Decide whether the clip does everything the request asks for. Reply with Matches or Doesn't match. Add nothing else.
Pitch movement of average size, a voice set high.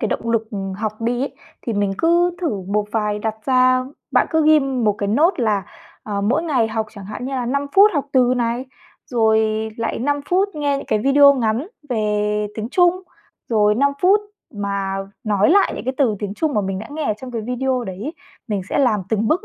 Matches